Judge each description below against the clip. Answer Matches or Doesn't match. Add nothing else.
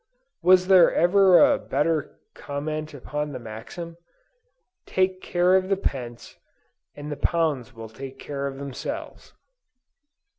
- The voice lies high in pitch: Doesn't match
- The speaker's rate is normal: Doesn't match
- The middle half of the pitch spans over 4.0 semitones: Matches